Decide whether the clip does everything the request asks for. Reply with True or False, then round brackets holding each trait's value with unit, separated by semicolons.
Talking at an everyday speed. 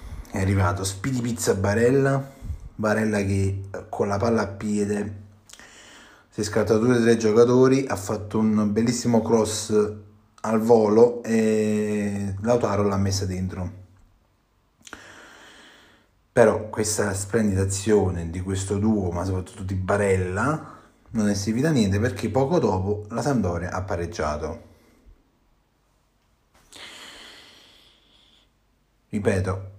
False (110 wpm)